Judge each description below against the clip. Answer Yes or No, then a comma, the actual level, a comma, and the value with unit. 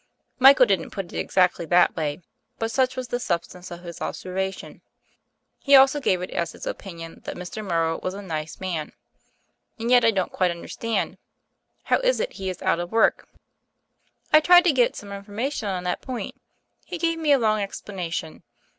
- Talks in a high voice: Yes, high, 195 Hz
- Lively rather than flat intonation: Yes, wide, 6.2 semitones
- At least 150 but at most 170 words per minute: No, average, 190 wpm